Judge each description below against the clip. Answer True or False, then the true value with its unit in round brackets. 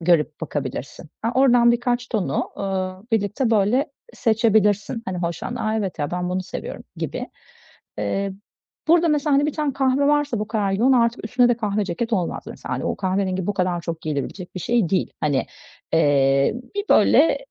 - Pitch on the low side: False (205 Hz)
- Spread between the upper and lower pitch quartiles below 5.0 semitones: False (5.4 semitones)